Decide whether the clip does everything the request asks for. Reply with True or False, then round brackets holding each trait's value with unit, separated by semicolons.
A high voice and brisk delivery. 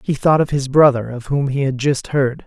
False (135 Hz; 265 wpm)